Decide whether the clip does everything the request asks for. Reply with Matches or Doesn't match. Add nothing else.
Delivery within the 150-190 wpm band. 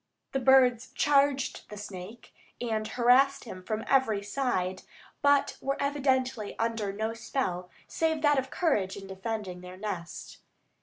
Doesn't match